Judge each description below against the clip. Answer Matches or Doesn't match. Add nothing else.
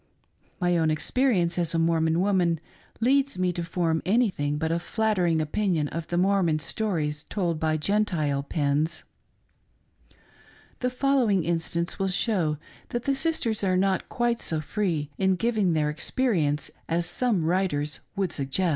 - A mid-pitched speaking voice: Matches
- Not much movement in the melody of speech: Doesn't match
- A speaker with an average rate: Matches